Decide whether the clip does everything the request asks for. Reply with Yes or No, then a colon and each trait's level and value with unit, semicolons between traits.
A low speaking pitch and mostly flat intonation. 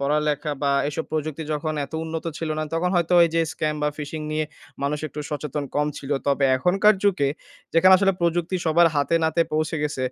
No: medium, 155 Hz; narrow, 2.1 semitones